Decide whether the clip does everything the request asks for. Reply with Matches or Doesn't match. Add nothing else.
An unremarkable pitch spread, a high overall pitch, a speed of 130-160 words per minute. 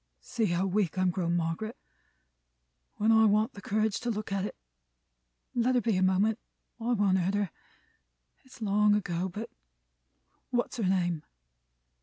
Matches